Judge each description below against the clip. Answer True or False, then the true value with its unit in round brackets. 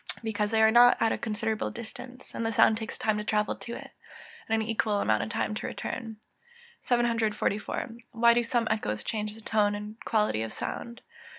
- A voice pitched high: True (220 Hz)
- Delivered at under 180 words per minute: False (185 wpm)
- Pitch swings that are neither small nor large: False (1.7 semitones)